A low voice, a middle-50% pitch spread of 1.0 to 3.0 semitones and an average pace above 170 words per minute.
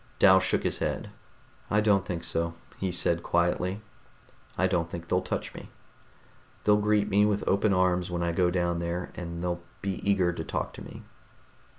Yes: very low, 90 Hz; narrow, 2.4 semitones; average, 185 wpm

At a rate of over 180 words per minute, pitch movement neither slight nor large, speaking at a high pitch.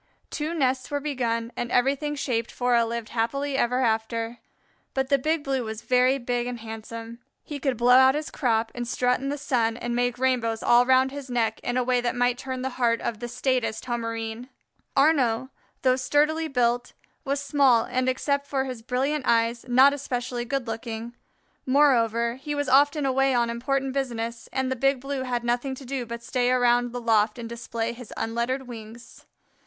No: average, 190 wpm; narrow, 2.3 semitones; very high, 250 Hz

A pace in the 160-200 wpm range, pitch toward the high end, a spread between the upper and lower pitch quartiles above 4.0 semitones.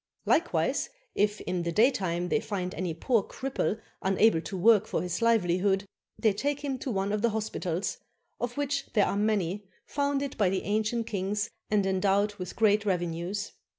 No: average, 170 wpm; high, 205 Hz; average, 3.3 semitones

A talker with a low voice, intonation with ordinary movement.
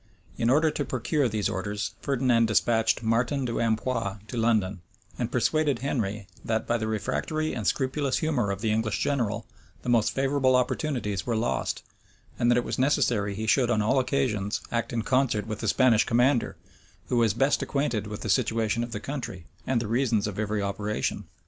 Yes: low, 115 Hz; average, 3.3 semitones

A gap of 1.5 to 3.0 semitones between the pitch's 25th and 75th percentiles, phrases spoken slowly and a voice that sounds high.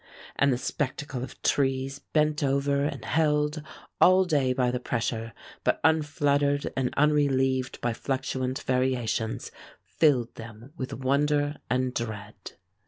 No: average, 2.7 semitones; slow, 125 wpm; low, 135 Hz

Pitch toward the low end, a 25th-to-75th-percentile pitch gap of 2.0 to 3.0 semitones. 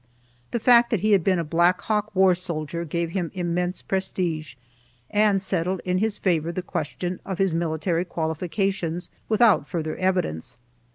No: medium, 180 Hz; narrow, 2.6 semitones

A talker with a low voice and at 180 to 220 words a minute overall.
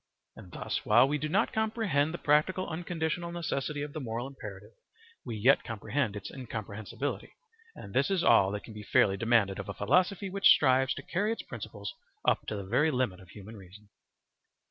Yes: low, 130 Hz; average, 190 wpm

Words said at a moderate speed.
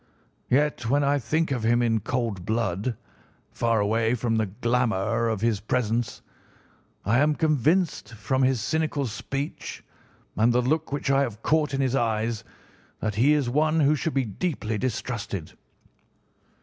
Yes: average, 155 wpm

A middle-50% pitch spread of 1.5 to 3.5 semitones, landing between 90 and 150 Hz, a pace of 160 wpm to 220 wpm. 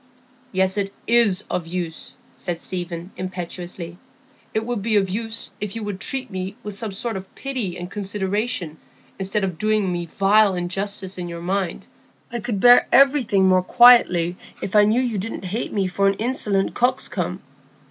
No: average, 3.0 semitones; high, 195 Hz; average, 170 wpm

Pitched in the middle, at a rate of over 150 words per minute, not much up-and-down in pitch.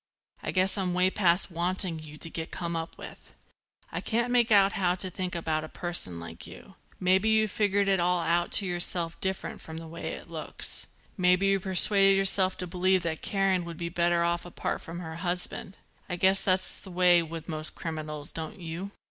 Yes: medium, 180 Hz; average, 200 wpm; narrow, 2.2 semitones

